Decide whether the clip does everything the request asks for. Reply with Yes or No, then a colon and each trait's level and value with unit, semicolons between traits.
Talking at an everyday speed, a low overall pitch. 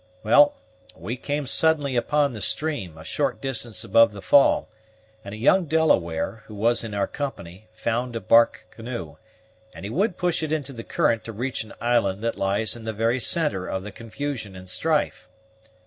Yes: average, 180 wpm; low, 115 Hz